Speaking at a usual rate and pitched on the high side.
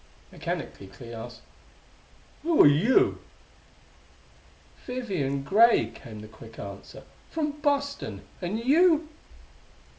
No: slow, 95 wpm; high, 210 Hz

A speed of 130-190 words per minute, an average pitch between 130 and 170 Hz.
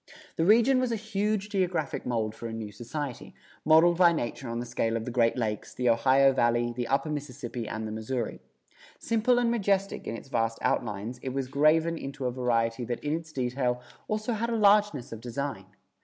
No: average, 200 wpm; low, 135 Hz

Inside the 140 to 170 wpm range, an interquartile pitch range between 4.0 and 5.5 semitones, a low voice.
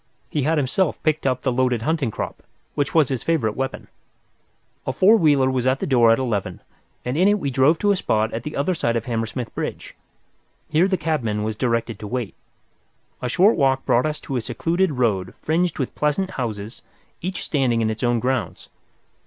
No: average, 200 wpm; average, 5.1 semitones; low, 130 Hz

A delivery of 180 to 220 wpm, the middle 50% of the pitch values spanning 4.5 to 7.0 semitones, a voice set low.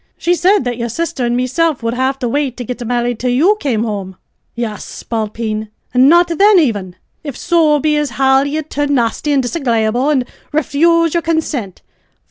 No: average, 185 wpm; average, 4.8 semitones; very high, 265 Hz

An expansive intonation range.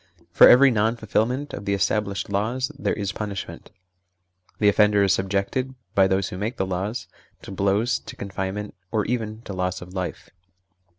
No: narrow, 2.6 semitones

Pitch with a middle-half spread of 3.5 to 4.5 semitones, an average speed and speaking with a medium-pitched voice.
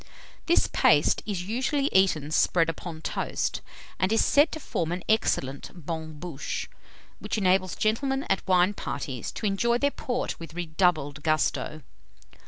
No: wide, 5.6 semitones; average, 145 wpm; medium, 180 Hz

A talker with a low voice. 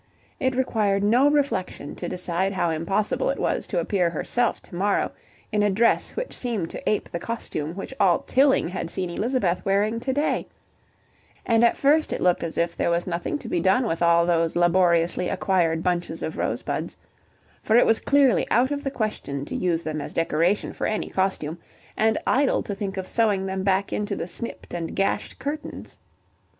No: high, 195 Hz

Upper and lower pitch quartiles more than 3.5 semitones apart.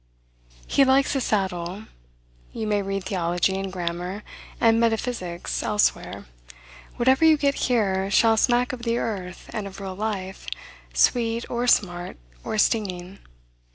Yes: average, 4.0 semitones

